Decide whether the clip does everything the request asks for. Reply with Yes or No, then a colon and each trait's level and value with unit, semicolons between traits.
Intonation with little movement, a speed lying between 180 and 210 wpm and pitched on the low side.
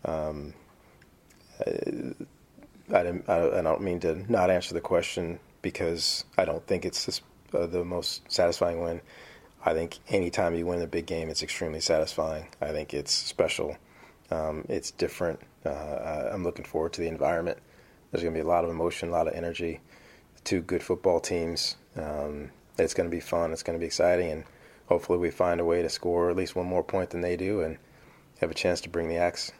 Yes: narrow, 1.6 semitones; average, 195 wpm; very low, 85 Hz